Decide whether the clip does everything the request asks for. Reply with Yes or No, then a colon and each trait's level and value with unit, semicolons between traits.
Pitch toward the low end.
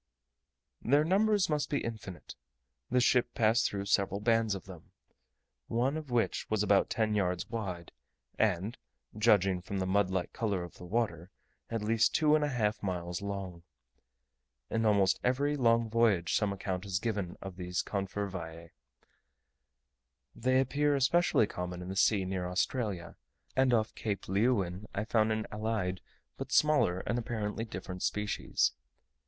Yes: low, 105 Hz